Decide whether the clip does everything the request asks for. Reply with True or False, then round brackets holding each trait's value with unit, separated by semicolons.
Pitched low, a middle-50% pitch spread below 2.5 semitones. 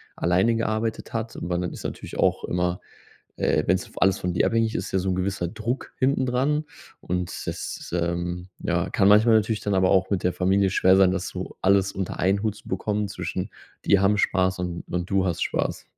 False (95 Hz; 2.8 semitones)